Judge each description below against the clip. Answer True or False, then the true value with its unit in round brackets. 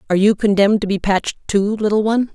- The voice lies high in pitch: True (205 Hz)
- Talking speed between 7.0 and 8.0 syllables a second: True (7.3 syllables/s)